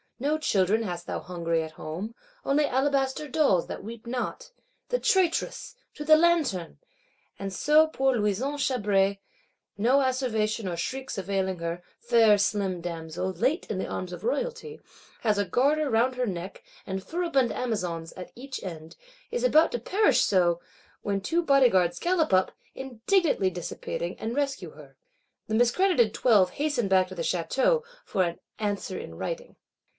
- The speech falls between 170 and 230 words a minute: No, average, 150 wpm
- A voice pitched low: No, high, 230 Hz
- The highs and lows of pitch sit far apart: Yes, wide, 7.6 semitones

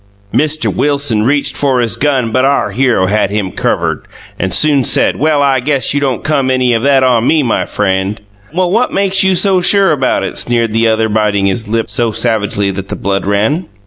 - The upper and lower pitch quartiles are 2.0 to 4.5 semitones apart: No, average, 5.1 semitones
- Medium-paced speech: No, fast, 210 wpm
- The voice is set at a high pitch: No, low, 125 Hz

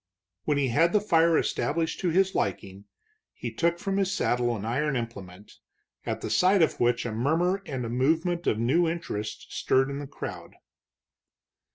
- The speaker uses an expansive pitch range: Yes, wide, 6.4 semitones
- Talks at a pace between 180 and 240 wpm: No, average, 170 wpm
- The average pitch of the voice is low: No, medium, 145 Hz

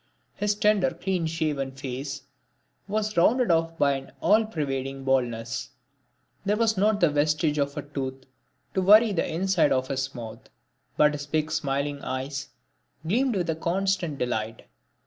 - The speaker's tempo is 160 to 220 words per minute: No, average, 150 wpm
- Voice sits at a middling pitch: Yes, medium, 150 Hz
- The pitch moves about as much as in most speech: No, wide, 5.9 semitones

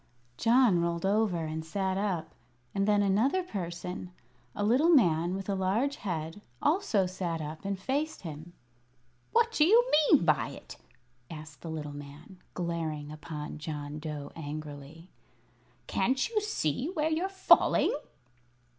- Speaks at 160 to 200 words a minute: No, average, 140 wpm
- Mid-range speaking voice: Yes, medium, 180 Hz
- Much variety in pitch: Yes, wide, 7.1 semitones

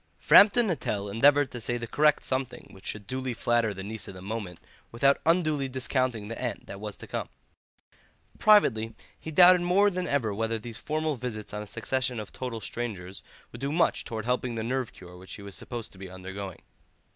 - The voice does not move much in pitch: No, average, 4.8 semitones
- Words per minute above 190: Yes, average, 200 wpm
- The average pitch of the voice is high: No, low, 120 Hz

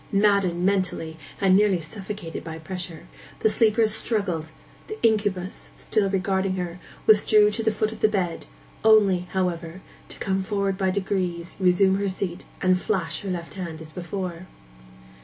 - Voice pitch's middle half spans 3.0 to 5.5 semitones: No, narrow, 2.6 semitones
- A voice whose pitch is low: No, high, 190 Hz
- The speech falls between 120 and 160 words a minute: Yes, average, 155 wpm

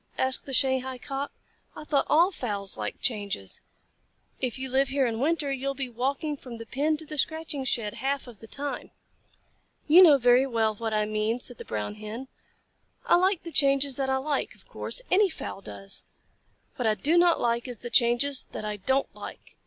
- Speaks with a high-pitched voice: Yes, very high, 265 Hz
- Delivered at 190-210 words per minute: Yes, average, 200 wpm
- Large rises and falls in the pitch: No, average, 3.7 semitones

